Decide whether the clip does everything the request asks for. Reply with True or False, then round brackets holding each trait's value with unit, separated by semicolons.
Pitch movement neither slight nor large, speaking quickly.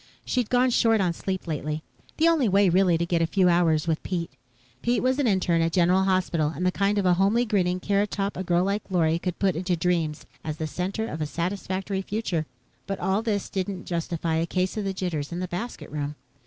True (3.0 semitones; 220 wpm)